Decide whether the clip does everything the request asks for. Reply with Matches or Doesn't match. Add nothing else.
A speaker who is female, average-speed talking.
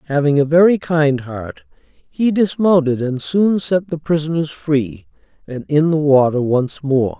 Doesn't match